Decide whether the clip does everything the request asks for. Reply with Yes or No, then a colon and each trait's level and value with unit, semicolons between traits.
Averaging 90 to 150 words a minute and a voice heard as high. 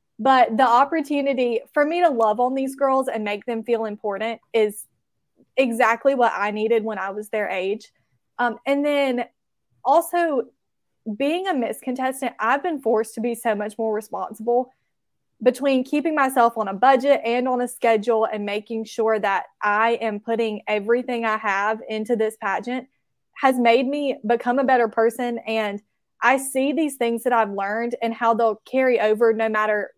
No: average, 175 wpm; high, 235 Hz